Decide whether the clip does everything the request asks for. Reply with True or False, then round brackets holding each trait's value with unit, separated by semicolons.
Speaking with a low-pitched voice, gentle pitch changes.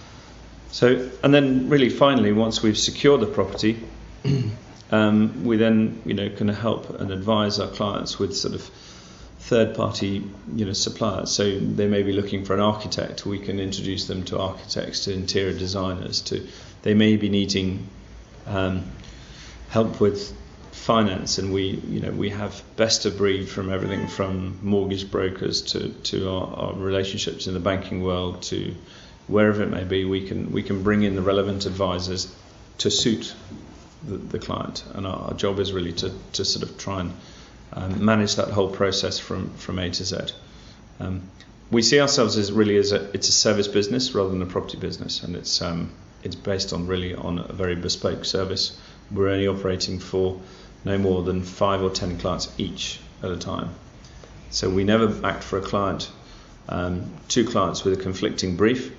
True (100 Hz; 2.0 semitones)